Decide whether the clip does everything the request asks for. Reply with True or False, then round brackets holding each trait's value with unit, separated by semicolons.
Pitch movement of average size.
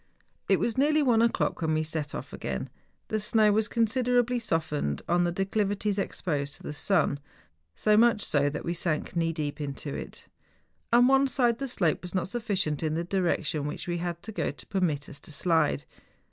False (6.3 semitones)